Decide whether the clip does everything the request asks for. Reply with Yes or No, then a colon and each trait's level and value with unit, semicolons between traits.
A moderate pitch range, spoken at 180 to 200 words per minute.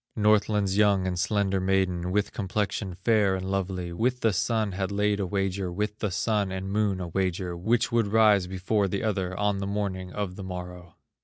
No: narrow, 2.1 semitones; average, 190 wpm